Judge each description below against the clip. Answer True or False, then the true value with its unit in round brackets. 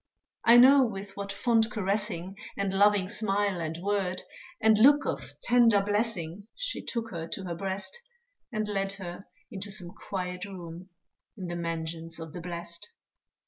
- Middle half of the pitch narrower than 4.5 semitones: True (3.3 semitones)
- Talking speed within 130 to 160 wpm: True (155 wpm)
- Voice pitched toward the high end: True (195 Hz)